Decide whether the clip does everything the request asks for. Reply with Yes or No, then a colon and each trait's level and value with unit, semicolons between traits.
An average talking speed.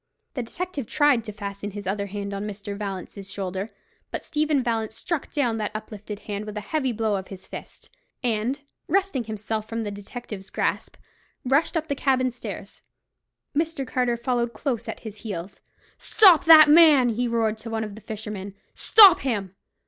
Yes: average, 175 wpm